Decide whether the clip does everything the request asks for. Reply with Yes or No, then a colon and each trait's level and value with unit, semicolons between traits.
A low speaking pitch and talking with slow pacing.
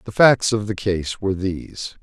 No: low, 100 Hz; fast, 205 wpm